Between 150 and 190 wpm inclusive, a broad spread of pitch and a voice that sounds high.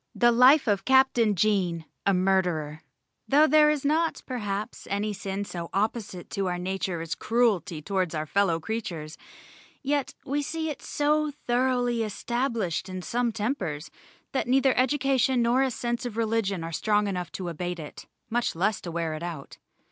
Yes: average, 165 wpm; wide, 6.0 semitones; high, 210 Hz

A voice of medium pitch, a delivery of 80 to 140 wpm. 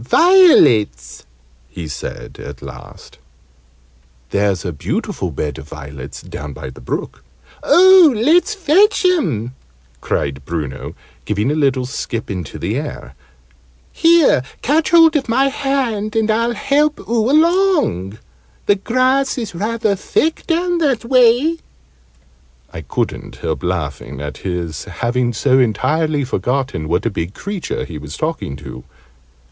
Yes: medium, 150 Hz; slow, 135 wpm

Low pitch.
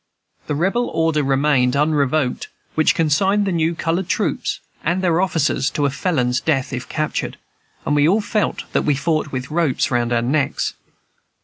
No: medium, 155 Hz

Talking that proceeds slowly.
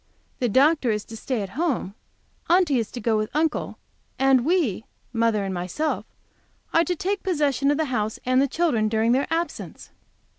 No: average, 175 wpm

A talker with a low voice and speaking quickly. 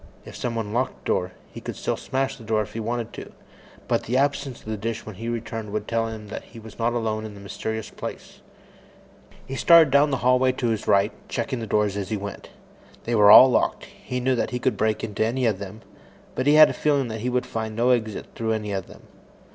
Yes: low, 115 Hz; fast, 245 wpm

